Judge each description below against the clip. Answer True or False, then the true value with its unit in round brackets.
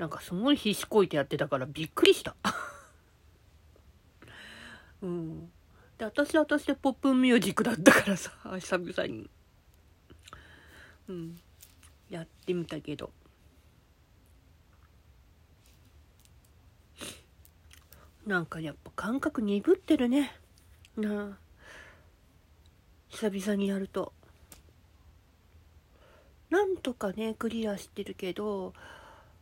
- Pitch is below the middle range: False (145 Hz)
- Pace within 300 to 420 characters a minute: False (190 characters per minute)